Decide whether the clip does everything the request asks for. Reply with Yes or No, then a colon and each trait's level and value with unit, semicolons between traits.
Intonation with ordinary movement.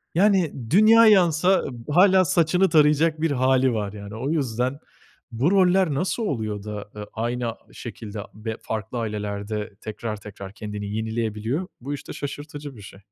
No: wide, 7.3 semitones